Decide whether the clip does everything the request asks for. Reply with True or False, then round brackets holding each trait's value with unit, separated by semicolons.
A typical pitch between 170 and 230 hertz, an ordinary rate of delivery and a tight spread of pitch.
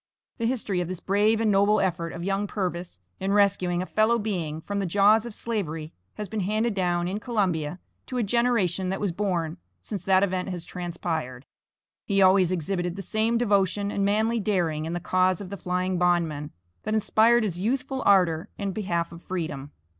False (190 Hz; 190 wpm; 3.1 semitones)